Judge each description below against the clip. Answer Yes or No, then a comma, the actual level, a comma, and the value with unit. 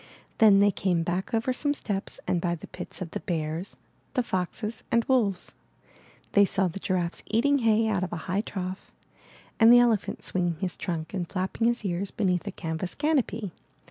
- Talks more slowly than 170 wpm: No, average, 185 wpm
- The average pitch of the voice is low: No, high, 195 Hz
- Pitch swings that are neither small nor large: Yes, average, 4.1 semitones